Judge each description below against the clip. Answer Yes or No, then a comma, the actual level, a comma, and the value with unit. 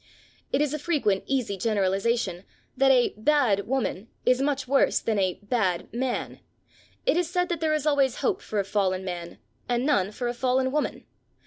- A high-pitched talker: Yes, high, 245 Hz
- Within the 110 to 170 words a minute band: No, average, 185 wpm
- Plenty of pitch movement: Yes, wide, 6.0 semitones